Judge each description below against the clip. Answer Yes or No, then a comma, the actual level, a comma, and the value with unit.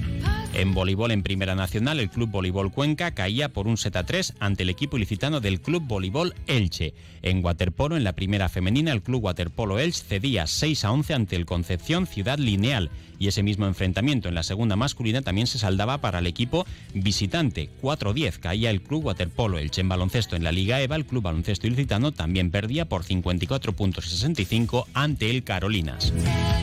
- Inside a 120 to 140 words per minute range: No, average, 185 wpm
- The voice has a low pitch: Yes, low, 100 Hz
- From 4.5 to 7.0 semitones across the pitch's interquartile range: Yes, average, 5.3 semitones